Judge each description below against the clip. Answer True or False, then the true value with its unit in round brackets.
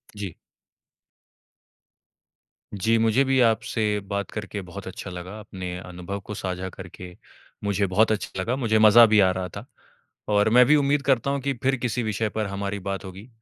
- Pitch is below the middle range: True (105 Hz)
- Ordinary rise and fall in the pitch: True (3.4 semitones)